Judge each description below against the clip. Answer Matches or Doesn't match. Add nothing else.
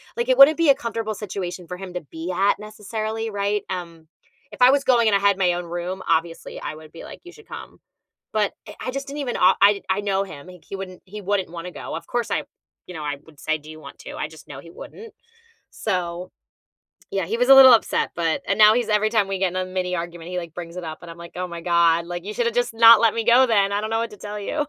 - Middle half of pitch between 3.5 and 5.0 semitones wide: Matches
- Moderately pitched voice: Doesn't match